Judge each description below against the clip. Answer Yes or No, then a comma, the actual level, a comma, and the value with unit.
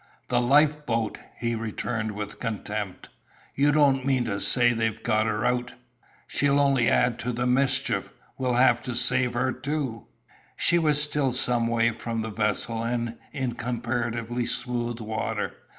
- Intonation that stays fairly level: Yes, narrow, 2.3 semitones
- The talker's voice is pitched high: No, low, 120 Hz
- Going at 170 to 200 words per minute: No, average, 155 wpm